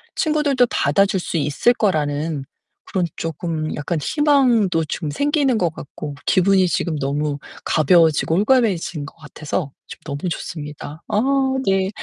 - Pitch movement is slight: No, wide, 5.5 semitones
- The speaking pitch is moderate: Yes, medium, 170 Hz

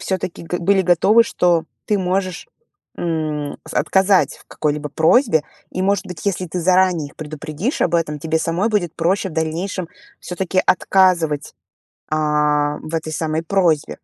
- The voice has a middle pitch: Yes, medium, 170 Hz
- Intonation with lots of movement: No, average, 3.2 semitones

